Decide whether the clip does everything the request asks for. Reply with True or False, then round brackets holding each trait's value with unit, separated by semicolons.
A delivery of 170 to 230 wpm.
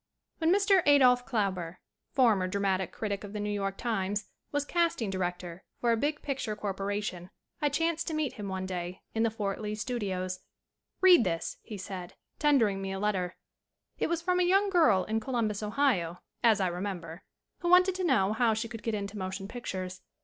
True (195 wpm)